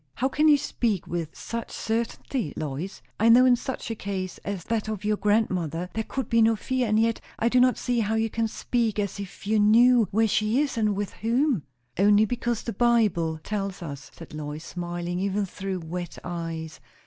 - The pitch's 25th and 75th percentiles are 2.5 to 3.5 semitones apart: No, average, 4.3 semitones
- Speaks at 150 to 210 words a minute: Yes, average, 200 wpm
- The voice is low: No, high, 210 Hz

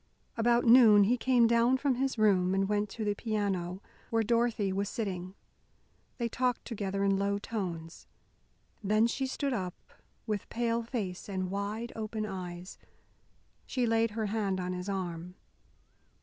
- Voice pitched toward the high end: Yes, high, 210 Hz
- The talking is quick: No, average, 150 wpm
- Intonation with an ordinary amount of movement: Yes, average, 3.3 semitones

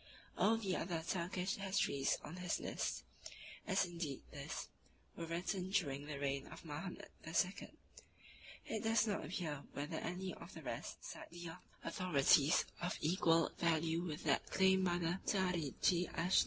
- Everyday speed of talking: Yes, average, 155 wpm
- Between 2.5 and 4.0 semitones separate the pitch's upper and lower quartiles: Yes, average, 3.0 semitones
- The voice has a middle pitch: Yes, medium, 175 Hz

